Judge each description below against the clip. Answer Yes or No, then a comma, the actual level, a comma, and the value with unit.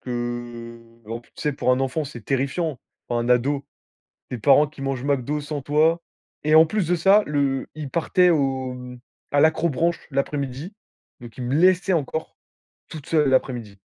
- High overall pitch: No, medium, 140 Hz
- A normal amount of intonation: Yes, average, 3.9 semitones